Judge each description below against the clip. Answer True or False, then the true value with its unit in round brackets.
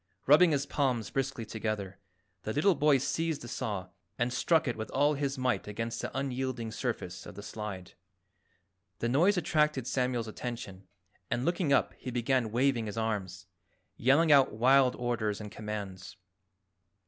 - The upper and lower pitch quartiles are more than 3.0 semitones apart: True (4.3 semitones)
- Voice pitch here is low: True (120 Hz)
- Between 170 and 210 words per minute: False (155 wpm)